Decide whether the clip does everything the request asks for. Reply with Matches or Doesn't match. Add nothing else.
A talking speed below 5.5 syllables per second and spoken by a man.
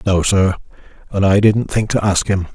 Matches